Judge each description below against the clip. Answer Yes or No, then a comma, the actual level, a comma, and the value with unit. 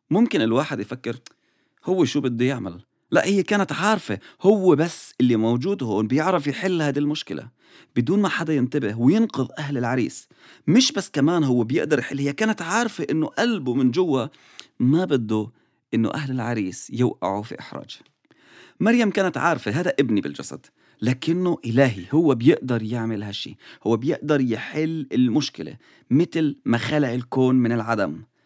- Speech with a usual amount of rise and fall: No, wide, 6.4 semitones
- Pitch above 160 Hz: No, medium, 140 Hz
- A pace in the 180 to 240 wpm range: No, average, 150 wpm